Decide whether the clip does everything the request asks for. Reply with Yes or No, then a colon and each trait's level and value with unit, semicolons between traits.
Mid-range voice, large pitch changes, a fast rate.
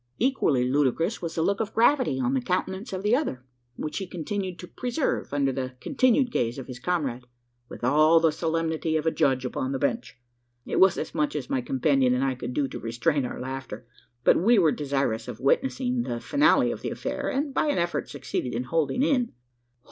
Yes: medium, 155 Hz; wide, 7.1 semitones; fast, 210 wpm